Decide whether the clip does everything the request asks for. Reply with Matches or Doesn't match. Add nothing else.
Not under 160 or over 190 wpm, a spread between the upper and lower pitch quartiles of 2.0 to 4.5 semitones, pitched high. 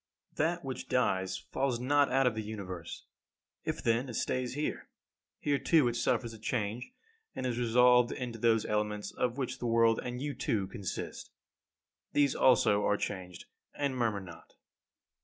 Doesn't match